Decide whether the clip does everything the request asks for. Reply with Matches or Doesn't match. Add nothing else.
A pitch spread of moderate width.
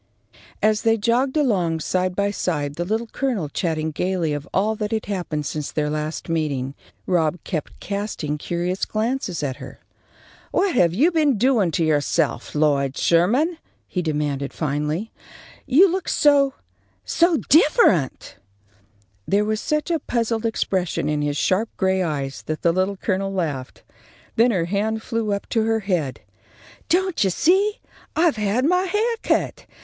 Doesn't match